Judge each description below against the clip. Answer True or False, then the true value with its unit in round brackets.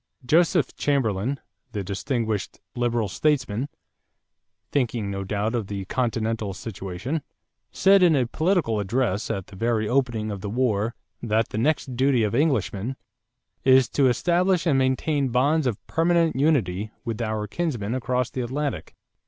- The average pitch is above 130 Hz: False (120 Hz)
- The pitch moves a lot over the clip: False (4.8 semitones)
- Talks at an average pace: True (145 wpm)